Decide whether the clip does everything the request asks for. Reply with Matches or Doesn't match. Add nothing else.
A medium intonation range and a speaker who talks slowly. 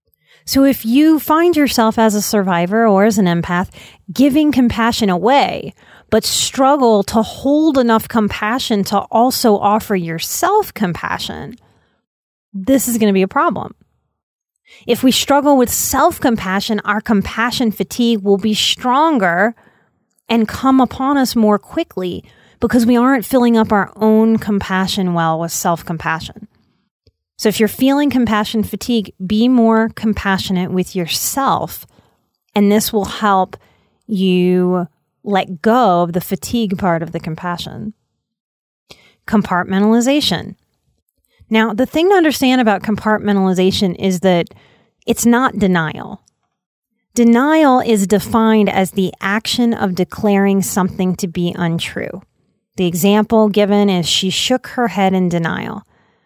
Matches